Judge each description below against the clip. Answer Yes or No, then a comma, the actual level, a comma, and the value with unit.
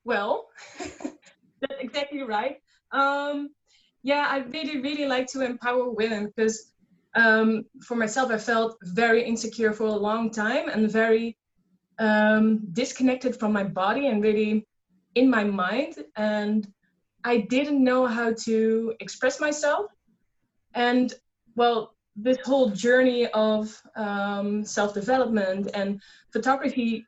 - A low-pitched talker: No, high, 225 Hz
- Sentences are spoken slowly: Yes, slow, 120 wpm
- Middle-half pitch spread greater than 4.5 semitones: No, average, 3.2 semitones